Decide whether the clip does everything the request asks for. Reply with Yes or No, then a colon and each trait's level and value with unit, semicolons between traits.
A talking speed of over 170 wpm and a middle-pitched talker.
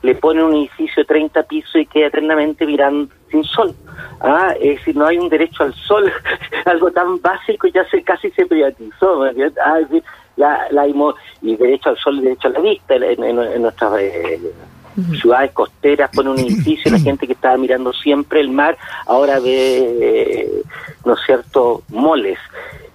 Yes: average, 185 wpm; medium, 170 Hz